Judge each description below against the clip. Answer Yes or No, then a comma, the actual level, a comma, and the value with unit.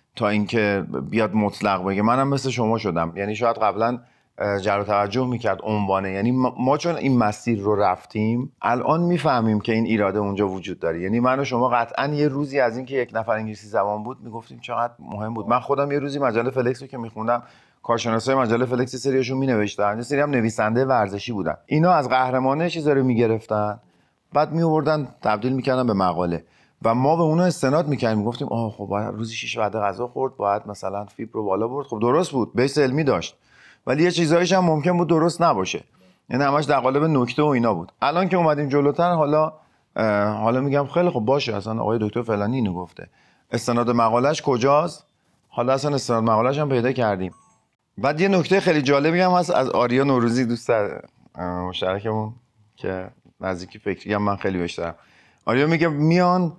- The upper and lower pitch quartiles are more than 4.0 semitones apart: Yes, average, 5.0 semitones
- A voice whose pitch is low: Yes, low, 120 Hz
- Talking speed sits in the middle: No, fast, 180 wpm